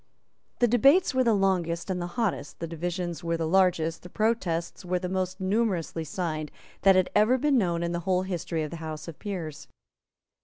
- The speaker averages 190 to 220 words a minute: Yes, average, 195 wpm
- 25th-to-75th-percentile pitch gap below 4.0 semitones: Yes, average, 2.8 semitones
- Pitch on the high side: No, medium, 180 Hz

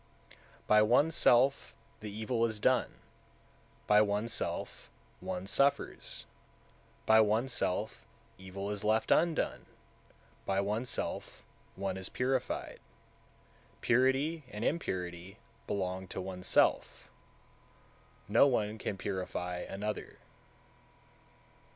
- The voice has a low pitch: Yes, low, 105 Hz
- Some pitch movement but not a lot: Yes, average, 4.2 semitones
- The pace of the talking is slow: Yes, slow, 90 wpm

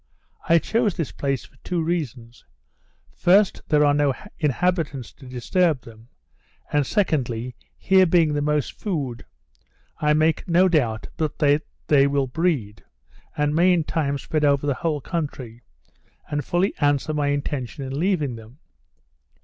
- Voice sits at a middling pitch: Yes, medium, 145 Hz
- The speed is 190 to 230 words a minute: No, average, 150 wpm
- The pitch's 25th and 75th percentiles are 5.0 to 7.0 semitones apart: No, average, 3.8 semitones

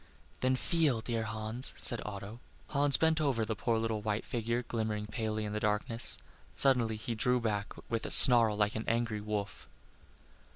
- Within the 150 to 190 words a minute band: Yes, average, 170 wpm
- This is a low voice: Yes, low, 115 Hz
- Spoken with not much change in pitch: Yes, narrow, 2.2 semitones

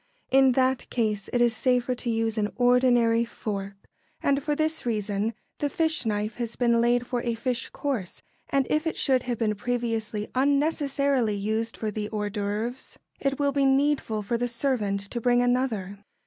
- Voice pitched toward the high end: Yes, high, 240 Hz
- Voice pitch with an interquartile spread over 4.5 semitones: No, average, 3.5 semitones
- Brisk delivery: No, average, 175 wpm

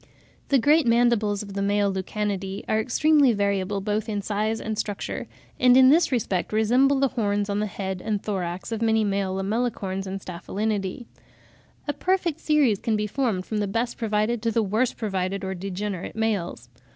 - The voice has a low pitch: No, high, 210 Hz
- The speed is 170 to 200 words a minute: Yes, average, 180 wpm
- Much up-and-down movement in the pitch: No, average, 3.0 semitones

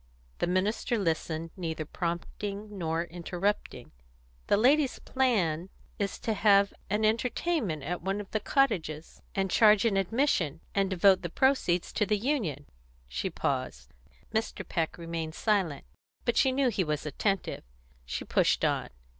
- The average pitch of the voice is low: No, high, 195 Hz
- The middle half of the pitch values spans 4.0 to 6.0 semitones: Yes, average, 4.7 semitones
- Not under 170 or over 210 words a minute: No, average, 145 wpm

